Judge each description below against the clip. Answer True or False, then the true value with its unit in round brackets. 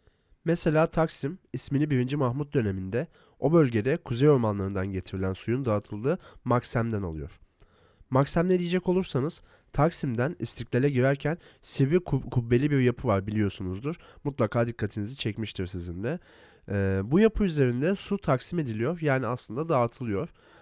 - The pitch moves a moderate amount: False (6.4 semitones)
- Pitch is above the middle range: False (125 Hz)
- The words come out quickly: False (130 wpm)